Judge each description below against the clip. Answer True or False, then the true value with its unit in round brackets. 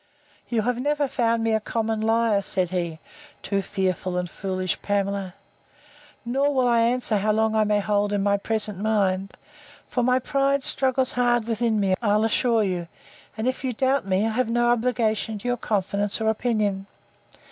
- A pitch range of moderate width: True (3.2 semitones)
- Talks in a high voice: True (220 Hz)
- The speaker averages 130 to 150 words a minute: False (180 wpm)